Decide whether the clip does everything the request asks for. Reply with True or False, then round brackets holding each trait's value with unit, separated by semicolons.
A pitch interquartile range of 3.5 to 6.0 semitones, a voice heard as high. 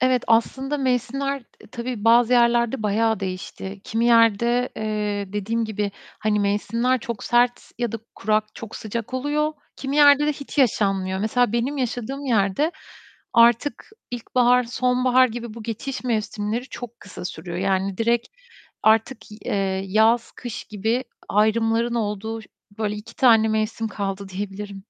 False (3.0 semitones; 230 Hz)